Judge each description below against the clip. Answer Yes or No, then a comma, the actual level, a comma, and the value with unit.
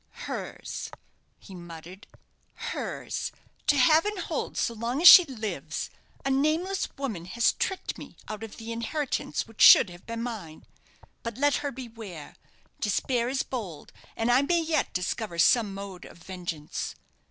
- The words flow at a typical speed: Yes, average, 155 wpm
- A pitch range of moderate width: No, wide, 6.4 semitones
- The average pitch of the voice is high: Yes, high, 230 Hz